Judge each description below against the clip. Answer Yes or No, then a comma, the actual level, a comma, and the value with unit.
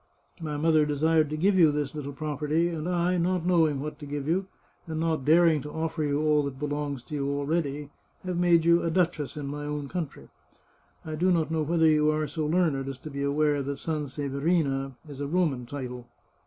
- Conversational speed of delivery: No, fast, 210 wpm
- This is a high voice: No, medium, 150 Hz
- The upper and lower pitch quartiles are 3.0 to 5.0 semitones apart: No, narrow, 2.4 semitones